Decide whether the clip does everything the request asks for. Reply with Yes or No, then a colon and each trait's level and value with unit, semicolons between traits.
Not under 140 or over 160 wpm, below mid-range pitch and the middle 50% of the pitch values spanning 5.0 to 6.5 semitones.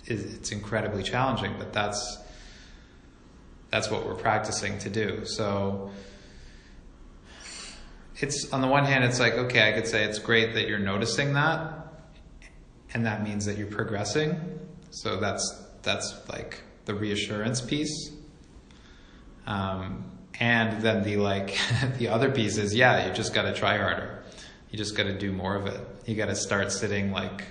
No: average, 150 wpm; low, 105 Hz; average, 2.8 semitones